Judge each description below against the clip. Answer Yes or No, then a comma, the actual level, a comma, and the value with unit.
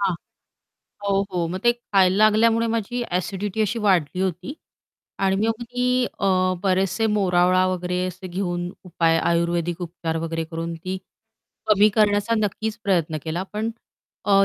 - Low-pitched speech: No, high, 190 Hz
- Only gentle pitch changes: No, average, 3.1 semitones